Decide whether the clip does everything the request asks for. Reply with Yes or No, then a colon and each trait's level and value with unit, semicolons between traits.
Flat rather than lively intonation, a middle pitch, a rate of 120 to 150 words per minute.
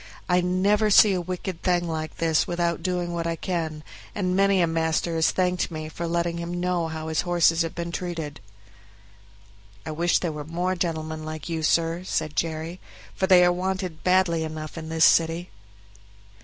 No: narrow, 2.0 semitones; medium, 170 Hz; average, 185 wpm